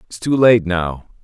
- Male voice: Yes, male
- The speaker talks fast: No, average, 195 wpm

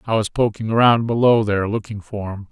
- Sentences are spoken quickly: Yes, fast, 215 wpm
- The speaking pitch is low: Yes, low, 110 Hz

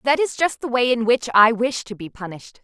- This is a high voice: Yes, high, 225 Hz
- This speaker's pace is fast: Yes, fast, 275 wpm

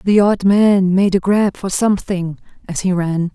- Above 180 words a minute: Yes, average, 200 wpm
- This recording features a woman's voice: Yes, female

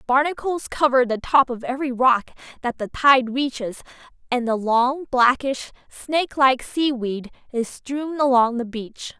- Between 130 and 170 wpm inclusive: Yes, average, 145 wpm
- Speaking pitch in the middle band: No, very high, 255 Hz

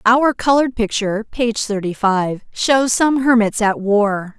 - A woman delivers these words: Yes, female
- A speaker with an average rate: Yes, average, 150 wpm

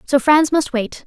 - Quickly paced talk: Yes, fast, 225 wpm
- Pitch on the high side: Yes, very high, 280 Hz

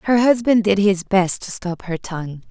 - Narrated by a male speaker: No, female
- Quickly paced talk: Yes, fast, 215 wpm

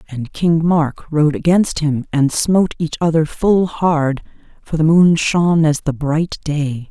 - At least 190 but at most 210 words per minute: No, average, 175 wpm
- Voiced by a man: No, female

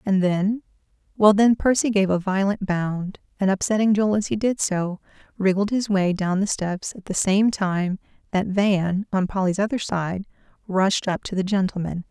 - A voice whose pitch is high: Yes, high, 195 Hz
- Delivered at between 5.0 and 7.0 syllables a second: No, 4.6 syllables/s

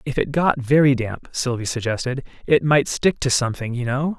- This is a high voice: No, low, 130 Hz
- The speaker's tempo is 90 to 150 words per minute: No, average, 200 wpm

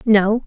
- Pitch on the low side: No, high, 210 Hz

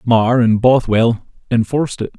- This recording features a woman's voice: No, male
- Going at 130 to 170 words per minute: Yes, slow, 135 wpm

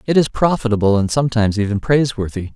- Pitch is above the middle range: No, low, 115 Hz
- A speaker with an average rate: Yes, average, 165 wpm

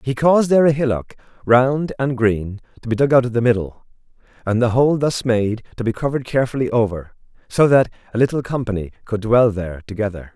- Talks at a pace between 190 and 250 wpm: Yes, average, 195 wpm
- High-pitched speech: No, low, 120 Hz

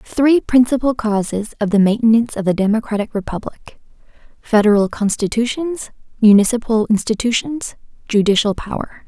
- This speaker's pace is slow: Yes, slow, 85 wpm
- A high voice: Yes, high, 225 Hz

